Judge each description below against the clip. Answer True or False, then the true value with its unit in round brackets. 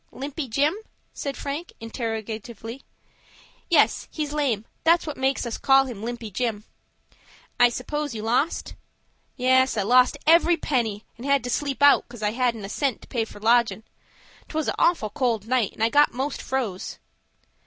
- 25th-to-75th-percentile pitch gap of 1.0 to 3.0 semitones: False (3.9 semitones)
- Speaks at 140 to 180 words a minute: True (165 wpm)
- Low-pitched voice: False (250 Hz)